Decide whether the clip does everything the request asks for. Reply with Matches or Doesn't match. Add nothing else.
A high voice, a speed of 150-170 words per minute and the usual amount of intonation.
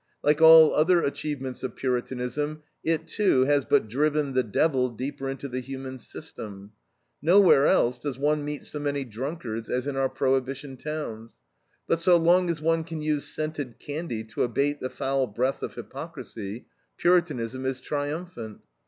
Doesn't match